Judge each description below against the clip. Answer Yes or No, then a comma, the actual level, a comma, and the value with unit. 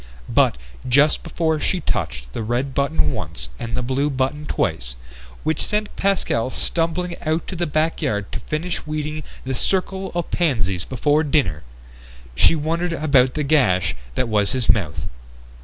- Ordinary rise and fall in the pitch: No, wide, 6.1 semitones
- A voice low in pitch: No, medium, 145 Hz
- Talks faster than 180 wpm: No, average, 155 wpm